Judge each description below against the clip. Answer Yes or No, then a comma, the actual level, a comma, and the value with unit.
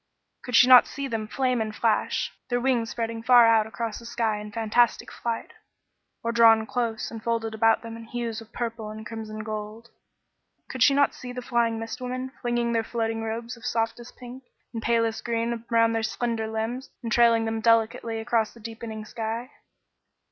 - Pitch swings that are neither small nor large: No, narrow, 1.2 semitones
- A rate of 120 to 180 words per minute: No, average, 190 wpm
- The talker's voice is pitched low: No, high, 230 Hz